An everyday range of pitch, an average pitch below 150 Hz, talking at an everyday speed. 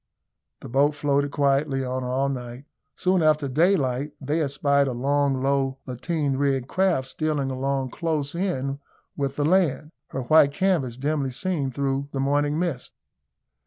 No: narrow, 2.3 semitones; medium, 140 Hz; average, 150 wpm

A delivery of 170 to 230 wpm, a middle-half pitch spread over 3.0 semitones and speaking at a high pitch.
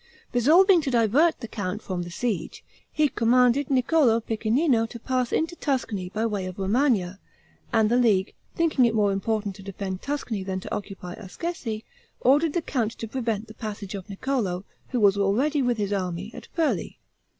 Yes: average, 175 wpm; average, 4.8 semitones; high, 225 Hz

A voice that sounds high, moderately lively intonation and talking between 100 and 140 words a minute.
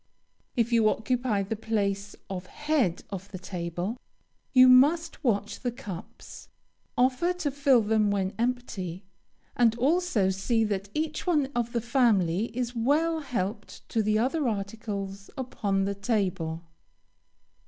Yes: high, 225 Hz; average, 4.4 semitones; slow, 135 wpm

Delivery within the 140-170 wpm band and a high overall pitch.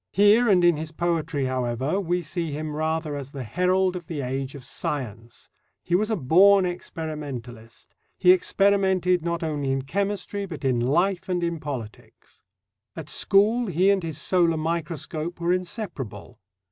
No: average, 160 wpm; medium, 165 Hz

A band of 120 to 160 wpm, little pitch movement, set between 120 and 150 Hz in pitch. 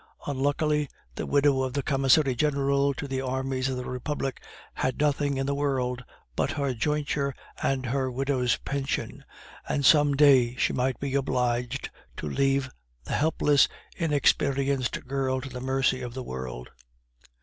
Yes: average, 150 wpm; narrow, 1.6 semitones; low, 135 Hz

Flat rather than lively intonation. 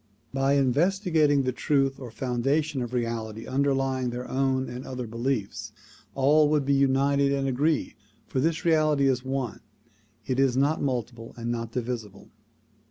Yes: narrow, 2.3 semitones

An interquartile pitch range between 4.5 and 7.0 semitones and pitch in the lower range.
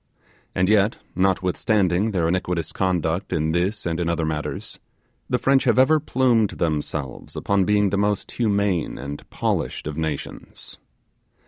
No: average, 4.1 semitones; very low, 95 Hz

